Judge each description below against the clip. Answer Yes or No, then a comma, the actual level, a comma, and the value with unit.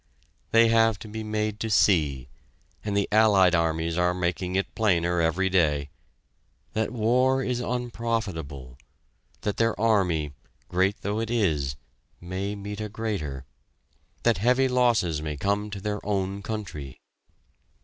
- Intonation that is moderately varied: Yes, average, 4.7 semitones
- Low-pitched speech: Yes, low, 100 Hz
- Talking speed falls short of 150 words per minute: Yes, average, 140 wpm